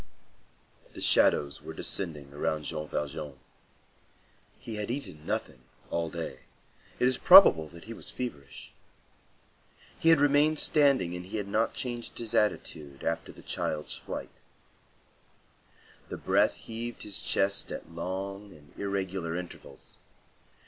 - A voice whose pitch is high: No, very low, 95 Hz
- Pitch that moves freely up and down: Yes, wide, 6.9 semitones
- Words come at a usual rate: No, slow, 130 wpm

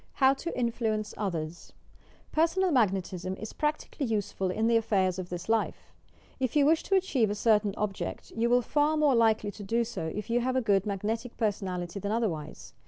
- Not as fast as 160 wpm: No, average, 190 wpm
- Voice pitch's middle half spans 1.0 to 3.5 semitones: No, average, 4.2 semitones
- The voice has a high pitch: Yes, high, 220 Hz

